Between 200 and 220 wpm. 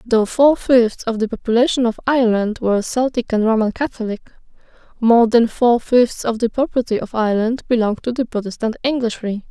No: average, 170 wpm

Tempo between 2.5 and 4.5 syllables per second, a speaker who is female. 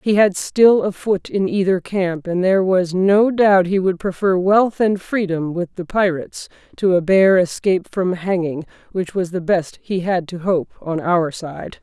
Yes: 4.3 syllables/s; female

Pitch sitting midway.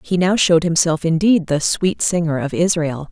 Yes: medium, 170 Hz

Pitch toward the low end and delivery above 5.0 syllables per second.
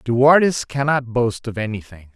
No: low, 125 Hz; 4.8 syllables/s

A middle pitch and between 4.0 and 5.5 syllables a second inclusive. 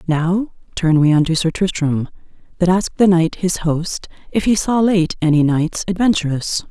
Yes: medium, 175 Hz; 4.7 syllables/s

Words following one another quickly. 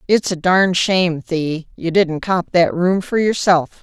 No: average, 190 wpm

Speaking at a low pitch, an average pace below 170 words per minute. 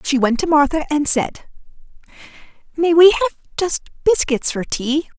No: very high, 305 Hz; average, 150 wpm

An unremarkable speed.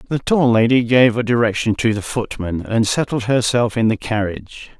Yes: average, 190 wpm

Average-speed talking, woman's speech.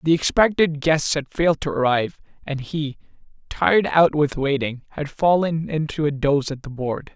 No: average, 175 wpm; male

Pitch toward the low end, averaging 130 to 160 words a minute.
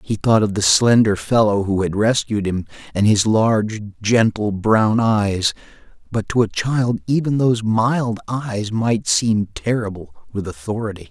Yes: low, 110 Hz; average, 155 wpm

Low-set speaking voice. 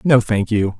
Yes: low, 110 Hz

